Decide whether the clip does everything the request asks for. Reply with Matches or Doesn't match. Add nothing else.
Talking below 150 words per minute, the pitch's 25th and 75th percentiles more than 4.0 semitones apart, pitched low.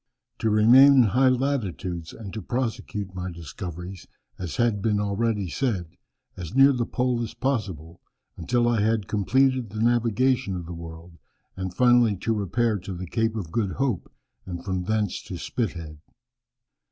Doesn't match